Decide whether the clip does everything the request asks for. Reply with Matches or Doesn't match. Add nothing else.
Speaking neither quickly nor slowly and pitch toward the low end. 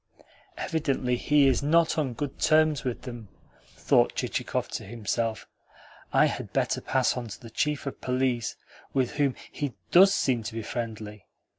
Matches